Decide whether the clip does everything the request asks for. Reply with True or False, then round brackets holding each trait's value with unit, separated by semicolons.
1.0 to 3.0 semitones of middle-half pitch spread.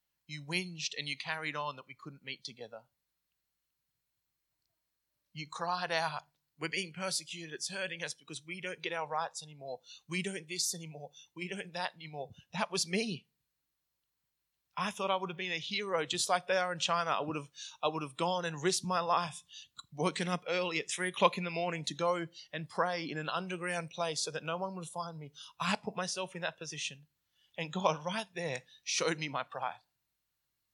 True (2.7 semitones)